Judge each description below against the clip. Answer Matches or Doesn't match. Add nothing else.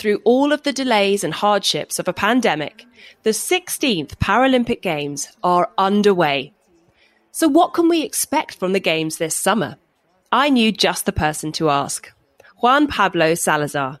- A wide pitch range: Matches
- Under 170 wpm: Matches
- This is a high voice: Matches